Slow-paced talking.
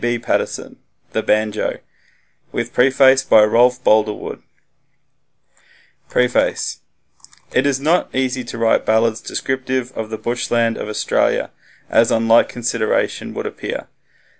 Yes: slow, 125 wpm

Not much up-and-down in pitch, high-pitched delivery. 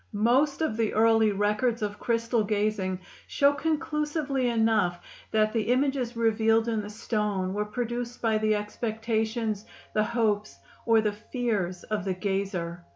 Yes: narrow, 2.3 semitones; high, 220 Hz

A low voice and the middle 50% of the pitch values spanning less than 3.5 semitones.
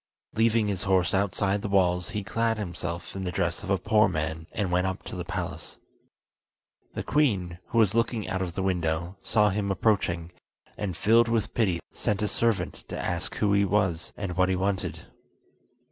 Yes: very low, 95 Hz; average, 3.0 semitones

